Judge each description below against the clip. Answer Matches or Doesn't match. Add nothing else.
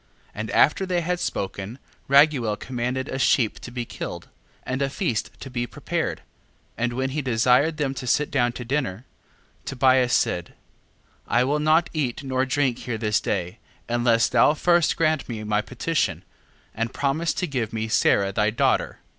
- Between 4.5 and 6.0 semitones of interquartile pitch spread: Doesn't match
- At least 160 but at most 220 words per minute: Matches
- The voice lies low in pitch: Matches